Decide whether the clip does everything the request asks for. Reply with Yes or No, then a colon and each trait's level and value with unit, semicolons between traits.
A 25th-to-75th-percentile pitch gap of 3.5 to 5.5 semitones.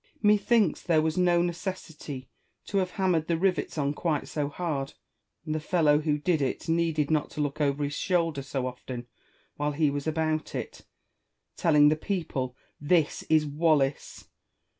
No: average, 2.8 semitones